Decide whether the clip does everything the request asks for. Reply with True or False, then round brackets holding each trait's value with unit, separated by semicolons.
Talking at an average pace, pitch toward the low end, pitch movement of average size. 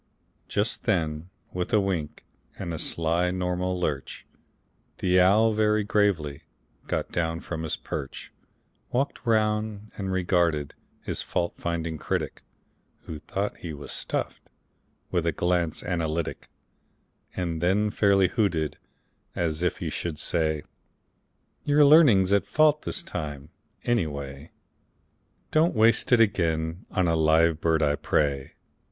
False (130 wpm; 85 Hz; 4.2 semitones)